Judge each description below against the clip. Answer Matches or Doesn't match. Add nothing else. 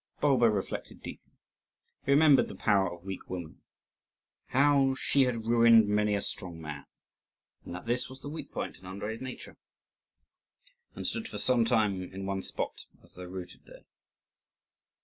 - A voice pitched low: Matches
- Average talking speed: Matches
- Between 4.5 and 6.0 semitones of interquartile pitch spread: Matches